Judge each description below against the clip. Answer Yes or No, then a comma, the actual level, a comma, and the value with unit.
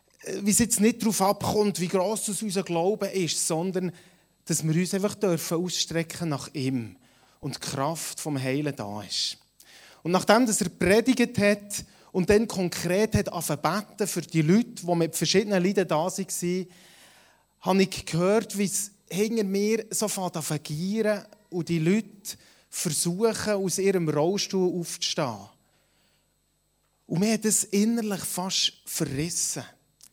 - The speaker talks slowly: No, average, 145 wpm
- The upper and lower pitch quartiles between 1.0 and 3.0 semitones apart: No, average, 3.6 semitones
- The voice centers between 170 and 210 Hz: Yes, medium, 185 Hz